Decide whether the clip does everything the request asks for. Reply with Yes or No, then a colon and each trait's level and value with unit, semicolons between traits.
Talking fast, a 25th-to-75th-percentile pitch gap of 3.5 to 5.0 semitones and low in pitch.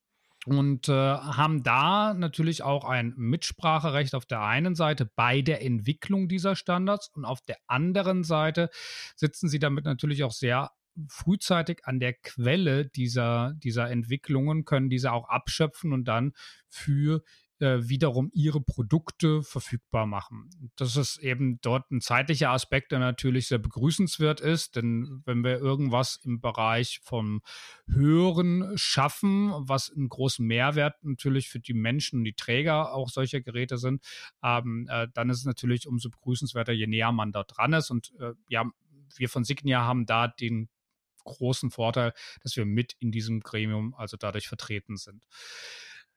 No: average, 150 wpm; average, 4.0 semitones; low, 130 Hz